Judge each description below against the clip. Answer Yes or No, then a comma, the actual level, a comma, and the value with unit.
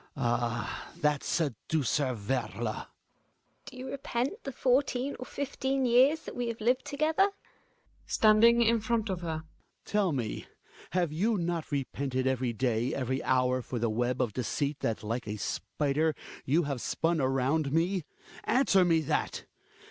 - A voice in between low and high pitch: Yes, medium, 160 Hz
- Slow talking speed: No, average, 155 wpm